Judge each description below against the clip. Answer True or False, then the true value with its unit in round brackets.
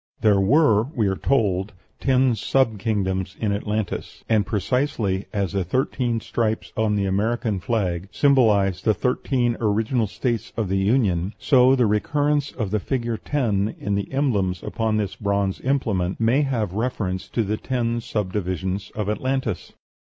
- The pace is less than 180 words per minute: True (150 wpm)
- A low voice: True (110 Hz)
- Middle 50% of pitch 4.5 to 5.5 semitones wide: False (4.0 semitones)